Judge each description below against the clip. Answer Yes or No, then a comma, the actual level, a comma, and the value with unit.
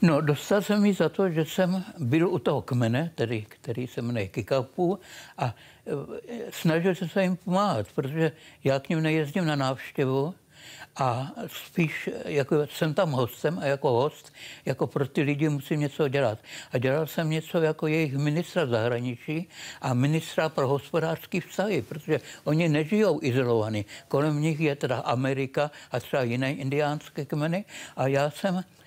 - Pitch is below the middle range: No, medium, 150 Hz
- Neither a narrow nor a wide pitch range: Yes, average, 3.6 semitones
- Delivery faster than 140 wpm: Yes, average, 160 wpm